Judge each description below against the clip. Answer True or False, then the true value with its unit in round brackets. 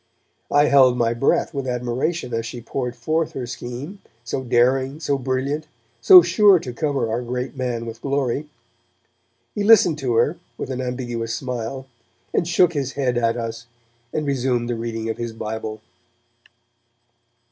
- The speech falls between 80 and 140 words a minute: False (160 wpm)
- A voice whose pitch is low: True (125 Hz)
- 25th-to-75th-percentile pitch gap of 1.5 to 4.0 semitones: True (3.1 semitones)